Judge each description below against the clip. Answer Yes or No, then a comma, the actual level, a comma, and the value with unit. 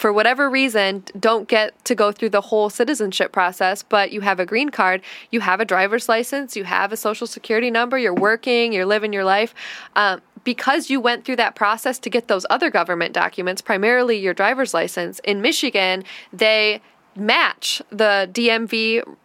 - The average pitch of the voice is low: No, high, 220 Hz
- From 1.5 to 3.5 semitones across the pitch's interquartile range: Yes, average, 3.1 semitones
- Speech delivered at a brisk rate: No, average, 180 wpm